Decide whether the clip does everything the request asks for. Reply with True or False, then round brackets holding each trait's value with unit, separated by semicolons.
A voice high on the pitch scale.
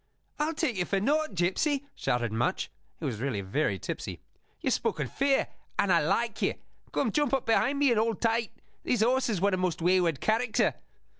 True (215 Hz)